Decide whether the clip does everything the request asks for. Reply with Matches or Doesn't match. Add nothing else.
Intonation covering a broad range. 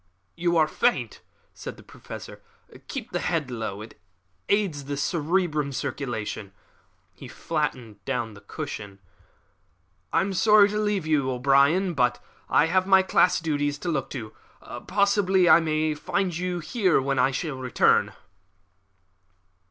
Matches